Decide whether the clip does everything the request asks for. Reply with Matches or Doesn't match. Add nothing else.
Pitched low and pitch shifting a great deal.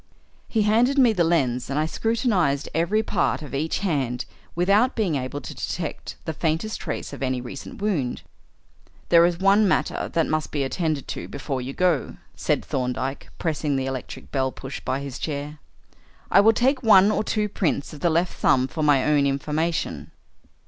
Doesn't match